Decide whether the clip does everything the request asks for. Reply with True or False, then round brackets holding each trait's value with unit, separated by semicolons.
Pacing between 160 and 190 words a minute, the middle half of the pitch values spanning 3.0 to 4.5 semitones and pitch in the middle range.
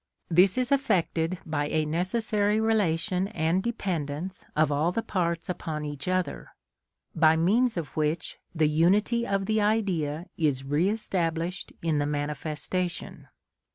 False (135 wpm; 4.2 semitones; 170 Hz)